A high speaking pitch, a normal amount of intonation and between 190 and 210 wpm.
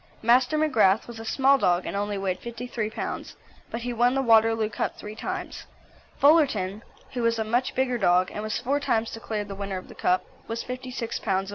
Yes: high, 225 Hz; average, 3.5 semitones; fast, 205 wpm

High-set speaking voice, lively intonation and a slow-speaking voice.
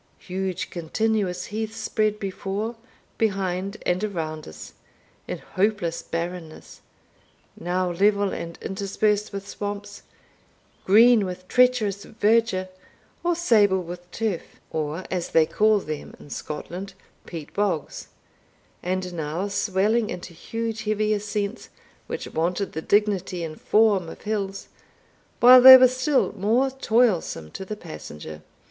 No: high, 200 Hz; average, 3.3 semitones; slow, 125 wpm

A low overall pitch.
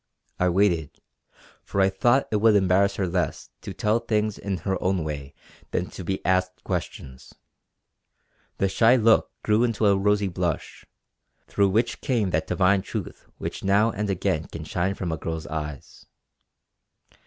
Yes: very low, 95 Hz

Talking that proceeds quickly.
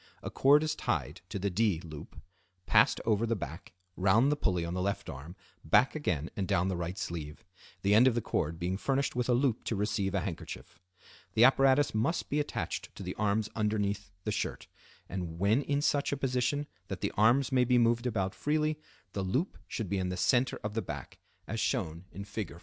Yes: fast, 210 wpm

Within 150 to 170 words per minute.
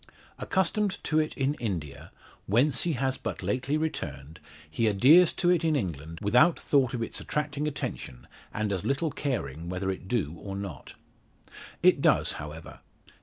Yes: average, 160 wpm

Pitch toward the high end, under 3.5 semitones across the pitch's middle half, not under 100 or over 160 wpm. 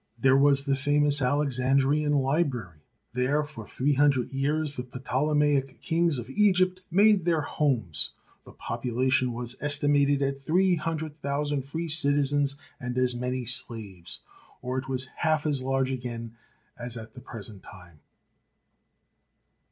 No: low, 135 Hz; average, 2.8 semitones; average, 140 wpm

